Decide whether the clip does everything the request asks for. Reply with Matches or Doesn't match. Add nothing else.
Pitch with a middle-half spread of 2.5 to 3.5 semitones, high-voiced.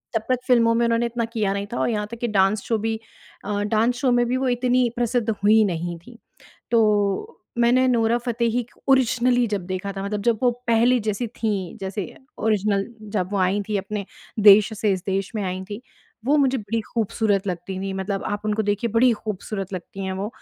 Matches